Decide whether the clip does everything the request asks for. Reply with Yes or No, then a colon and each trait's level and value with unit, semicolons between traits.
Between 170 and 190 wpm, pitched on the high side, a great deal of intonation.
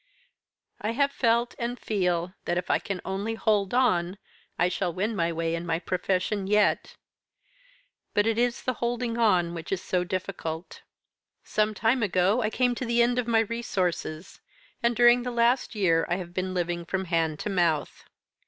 No: average, 180 wpm; high, 195 Hz; average, 5.0 semitones